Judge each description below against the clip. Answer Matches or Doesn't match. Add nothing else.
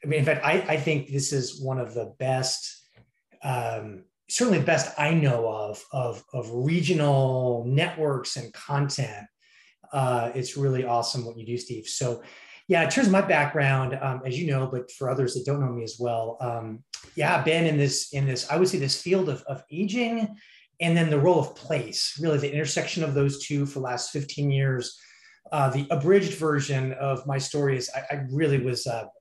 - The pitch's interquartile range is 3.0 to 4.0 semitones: Matches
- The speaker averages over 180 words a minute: Matches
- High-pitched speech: Doesn't match